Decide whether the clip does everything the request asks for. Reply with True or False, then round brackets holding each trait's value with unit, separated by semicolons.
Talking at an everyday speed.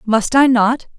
True (180 wpm)